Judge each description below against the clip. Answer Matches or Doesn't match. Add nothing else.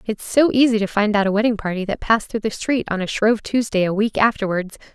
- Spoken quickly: Matches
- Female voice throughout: Matches